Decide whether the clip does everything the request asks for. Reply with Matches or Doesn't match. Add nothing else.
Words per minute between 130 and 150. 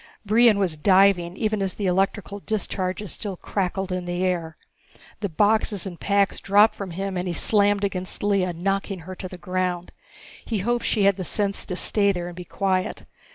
Doesn't match